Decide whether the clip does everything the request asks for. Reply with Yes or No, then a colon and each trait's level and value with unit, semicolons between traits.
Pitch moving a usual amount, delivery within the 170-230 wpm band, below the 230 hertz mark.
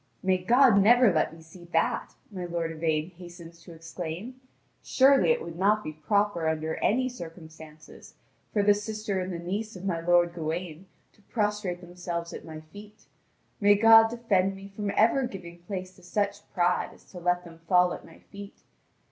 Yes: average, 3.6 semitones; average, 180 wpm; medium, 185 Hz